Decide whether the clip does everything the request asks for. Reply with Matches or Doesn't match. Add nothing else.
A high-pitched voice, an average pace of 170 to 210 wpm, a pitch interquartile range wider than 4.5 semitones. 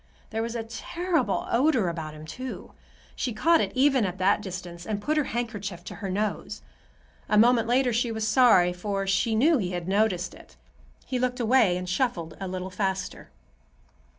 Matches